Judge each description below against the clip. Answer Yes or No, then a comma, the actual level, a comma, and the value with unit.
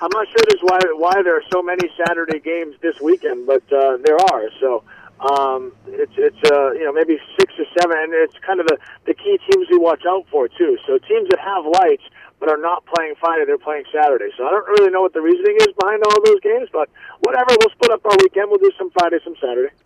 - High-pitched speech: Yes, high, 200 Hz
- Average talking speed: No, fast, 250 wpm